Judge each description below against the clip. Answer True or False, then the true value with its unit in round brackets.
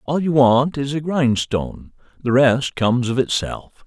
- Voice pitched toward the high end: False (130 Hz)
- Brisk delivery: False (170 wpm)